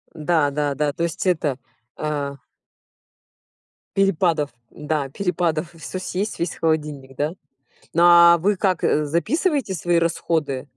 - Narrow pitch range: No, average, 3.0 semitones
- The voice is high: No, medium, 165 Hz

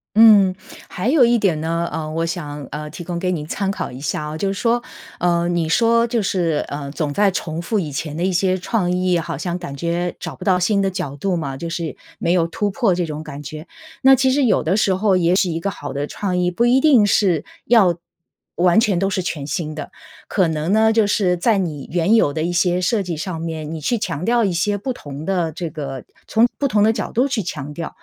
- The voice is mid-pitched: Yes, medium, 175 Hz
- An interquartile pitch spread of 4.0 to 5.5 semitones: Yes, average, 4.3 semitones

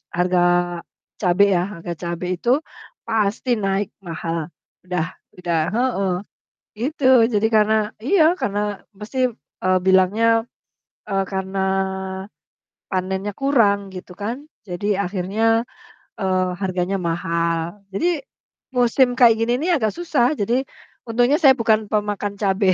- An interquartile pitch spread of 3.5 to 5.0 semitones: Yes, average, 4.3 semitones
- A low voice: No, high, 205 Hz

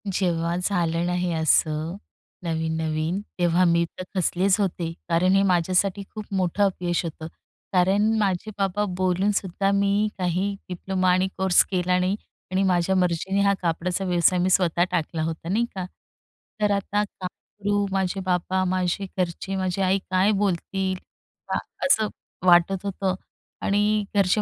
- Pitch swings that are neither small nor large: No, narrow, 2.1 semitones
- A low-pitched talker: No, medium, 185 Hz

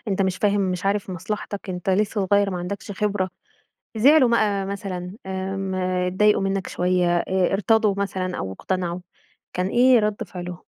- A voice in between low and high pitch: No, high, 195 Hz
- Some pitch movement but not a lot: No, narrow, 2.0 semitones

